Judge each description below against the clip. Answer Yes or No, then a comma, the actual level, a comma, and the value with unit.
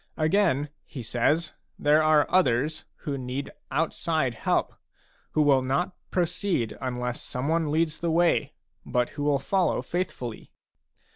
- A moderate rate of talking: No, slow, 130 wpm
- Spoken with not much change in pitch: No, average, 4.2 semitones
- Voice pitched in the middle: Yes, medium, 150 Hz